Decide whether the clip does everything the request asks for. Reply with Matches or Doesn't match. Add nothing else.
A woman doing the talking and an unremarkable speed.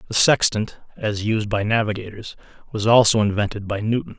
Doesn't match